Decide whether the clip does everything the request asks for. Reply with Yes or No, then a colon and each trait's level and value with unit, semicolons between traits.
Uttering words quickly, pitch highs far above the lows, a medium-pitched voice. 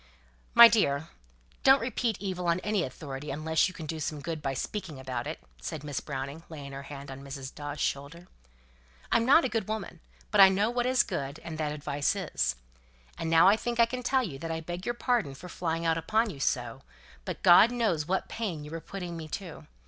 Yes: fast, 215 wpm; wide, 6.5 semitones; medium, 165 Hz